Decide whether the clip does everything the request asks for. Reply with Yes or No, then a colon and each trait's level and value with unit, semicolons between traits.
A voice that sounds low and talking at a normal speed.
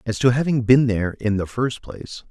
No: low, 115 Hz; fast, 235 wpm